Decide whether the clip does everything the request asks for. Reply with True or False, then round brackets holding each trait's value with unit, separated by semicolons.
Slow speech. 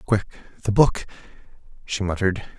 True (95 wpm)